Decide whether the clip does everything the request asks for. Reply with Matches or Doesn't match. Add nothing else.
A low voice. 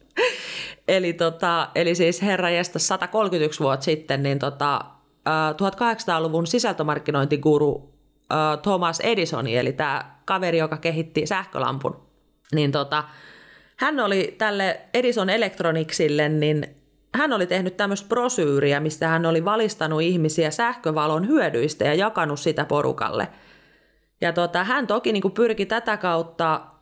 Doesn't match